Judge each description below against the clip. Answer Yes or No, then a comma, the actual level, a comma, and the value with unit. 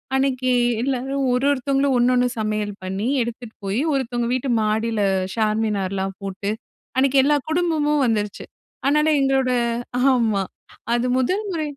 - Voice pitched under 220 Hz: No, very high, 250 Hz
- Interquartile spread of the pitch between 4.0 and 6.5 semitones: Yes, average, 4.3 semitones